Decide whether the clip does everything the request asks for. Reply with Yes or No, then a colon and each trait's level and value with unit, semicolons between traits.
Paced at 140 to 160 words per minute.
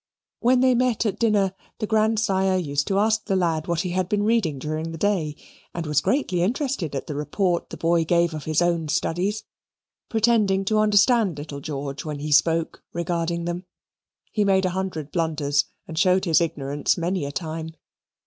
No: average, 185 wpm